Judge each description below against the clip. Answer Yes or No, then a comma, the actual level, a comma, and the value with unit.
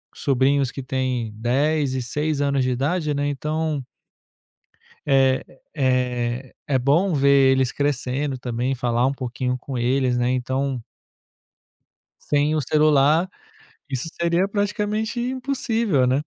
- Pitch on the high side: No, low, 135 Hz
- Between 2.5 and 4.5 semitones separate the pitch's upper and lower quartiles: Yes, average, 3.1 semitones